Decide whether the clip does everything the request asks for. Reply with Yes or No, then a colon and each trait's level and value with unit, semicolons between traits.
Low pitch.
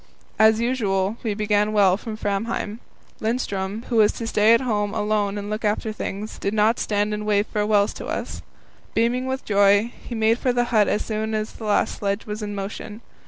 No: high, 215 Hz